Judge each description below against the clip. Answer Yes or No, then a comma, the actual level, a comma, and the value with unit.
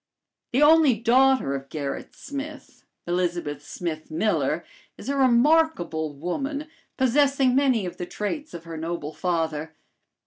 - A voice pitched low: No, high, 205 Hz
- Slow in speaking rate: Yes, slow, 130 wpm